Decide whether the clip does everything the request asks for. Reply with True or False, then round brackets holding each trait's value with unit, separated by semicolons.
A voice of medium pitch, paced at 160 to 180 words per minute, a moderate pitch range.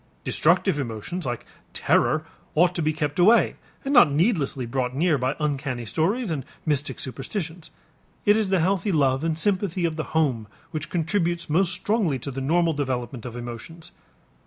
True (155 Hz; 165 wpm; 4.9 semitones)